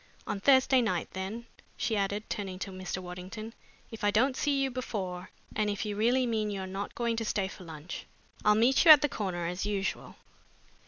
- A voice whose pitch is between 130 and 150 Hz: No, high, 210 Hz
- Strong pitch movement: No, average, 3.8 semitones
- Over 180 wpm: Yes, average, 200 wpm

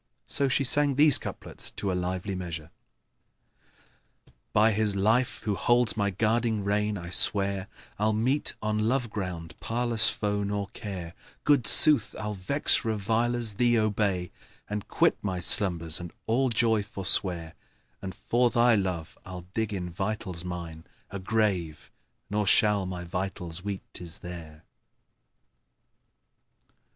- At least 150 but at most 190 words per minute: No, average, 140 wpm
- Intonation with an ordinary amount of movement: Yes, average, 3.6 semitones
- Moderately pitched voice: No, low, 100 Hz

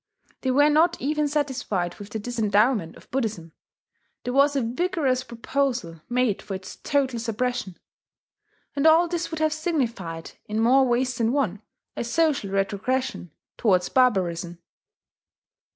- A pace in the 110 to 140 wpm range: Yes, slow, 135 wpm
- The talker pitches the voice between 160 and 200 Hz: No, high, 245 Hz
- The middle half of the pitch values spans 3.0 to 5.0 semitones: No, wide, 5.5 semitones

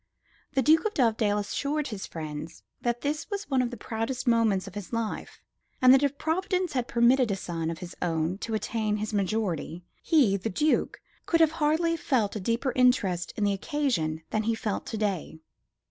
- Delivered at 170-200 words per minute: Yes, average, 190 wpm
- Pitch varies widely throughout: Yes, wide, 5.7 semitones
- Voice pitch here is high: Yes, high, 225 Hz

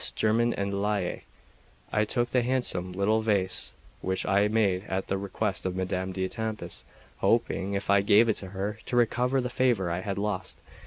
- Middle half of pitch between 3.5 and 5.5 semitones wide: No, average, 2.9 semitones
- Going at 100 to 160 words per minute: No, average, 175 wpm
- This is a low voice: Yes, low, 100 Hz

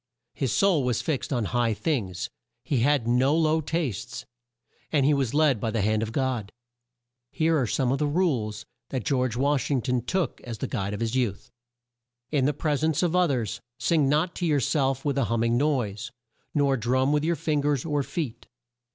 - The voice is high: No, low, 135 Hz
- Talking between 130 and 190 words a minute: No, fast, 205 wpm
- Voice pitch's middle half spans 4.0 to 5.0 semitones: Yes, average, 4.3 semitones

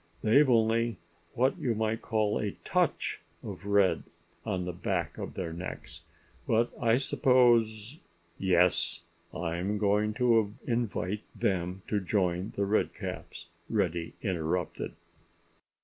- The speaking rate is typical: No, slow, 115 wpm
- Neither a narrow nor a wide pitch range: Yes, average, 3.8 semitones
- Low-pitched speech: Yes, low, 105 Hz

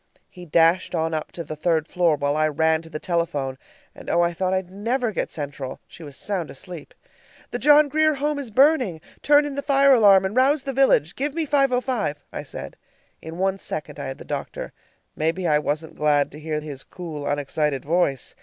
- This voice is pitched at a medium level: Yes, medium, 170 Hz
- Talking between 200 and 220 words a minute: Yes, fast, 205 wpm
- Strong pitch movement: Yes, wide, 8.8 semitones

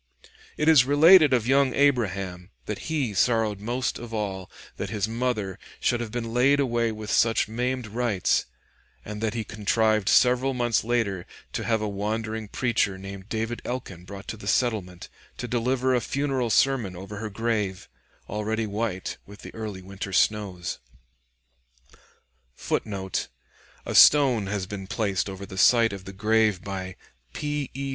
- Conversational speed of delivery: Yes, average, 155 wpm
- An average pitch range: Yes, average, 3.7 semitones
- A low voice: Yes, low, 110 Hz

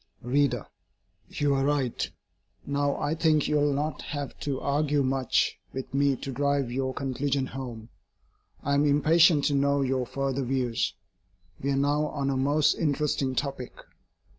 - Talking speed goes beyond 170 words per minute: No, average, 155 wpm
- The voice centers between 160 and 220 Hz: No, medium, 140 Hz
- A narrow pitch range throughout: Yes, narrow, 1.5 semitones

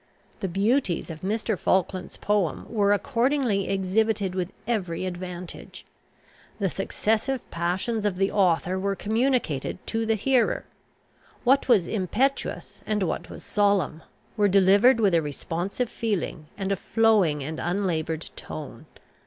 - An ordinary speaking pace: No, slow, 130 wpm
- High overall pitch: Yes, high, 200 Hz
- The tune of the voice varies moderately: Yes, average, 3.7 semitones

